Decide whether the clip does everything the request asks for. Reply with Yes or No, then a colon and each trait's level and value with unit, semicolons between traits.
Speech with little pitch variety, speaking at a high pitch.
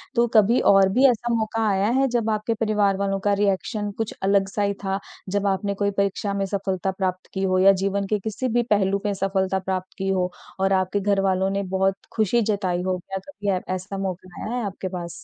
Yes: narrow, 1.6 semitones; high, 195 Hz